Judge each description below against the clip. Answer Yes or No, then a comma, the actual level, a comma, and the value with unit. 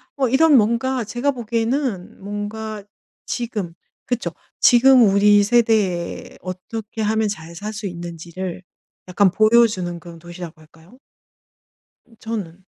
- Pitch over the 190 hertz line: Yes, high, 210 Hz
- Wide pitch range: No, average, 4.6 semitones